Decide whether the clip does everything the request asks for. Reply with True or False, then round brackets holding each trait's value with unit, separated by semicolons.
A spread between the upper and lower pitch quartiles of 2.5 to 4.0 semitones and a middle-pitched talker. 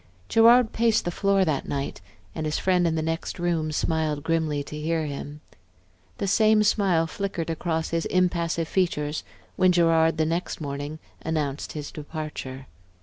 True (3.0 semitones; 165 Hz)